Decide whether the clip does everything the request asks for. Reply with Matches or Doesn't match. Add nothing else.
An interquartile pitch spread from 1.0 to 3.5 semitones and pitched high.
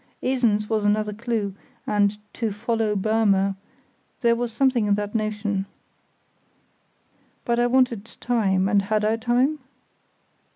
Matches